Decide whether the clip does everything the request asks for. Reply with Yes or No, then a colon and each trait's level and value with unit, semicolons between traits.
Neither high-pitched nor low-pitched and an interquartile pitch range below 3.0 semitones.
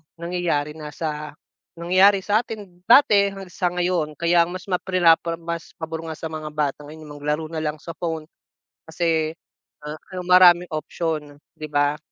Yes: medium, 165 Hz; narrow, 2.6 semitones